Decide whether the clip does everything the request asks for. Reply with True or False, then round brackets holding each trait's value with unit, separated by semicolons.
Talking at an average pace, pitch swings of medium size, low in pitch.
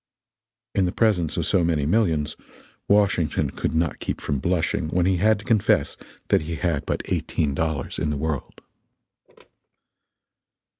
True (150 wpm; 3.9 semitones; 85 Hz)